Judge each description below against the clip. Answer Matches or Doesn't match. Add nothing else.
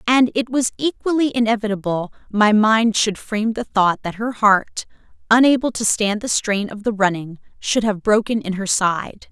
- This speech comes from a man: Doesn't match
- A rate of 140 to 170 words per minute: Doesn't match